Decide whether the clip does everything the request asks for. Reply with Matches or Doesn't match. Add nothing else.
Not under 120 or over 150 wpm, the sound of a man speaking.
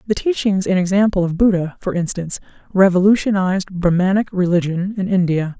Doesn't match